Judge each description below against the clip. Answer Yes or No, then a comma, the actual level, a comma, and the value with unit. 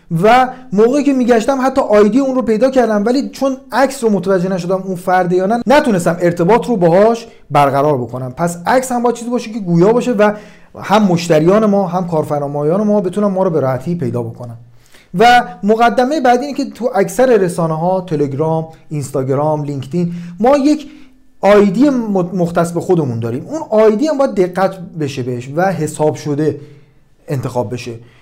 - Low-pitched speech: No, high, 190 Hz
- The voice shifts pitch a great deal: Yes, wide, 7.7 semitones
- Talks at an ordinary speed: No, fast, 170 wpm